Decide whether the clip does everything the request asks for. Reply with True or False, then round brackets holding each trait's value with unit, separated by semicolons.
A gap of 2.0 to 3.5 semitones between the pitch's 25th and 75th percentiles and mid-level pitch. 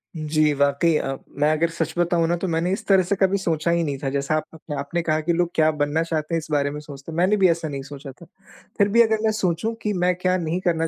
True (2.8 semitones; 165 Hz)